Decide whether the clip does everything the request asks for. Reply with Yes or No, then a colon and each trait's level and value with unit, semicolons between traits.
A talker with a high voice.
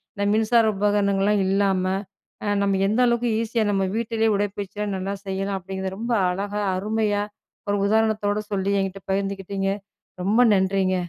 Yes: high, 200 Hz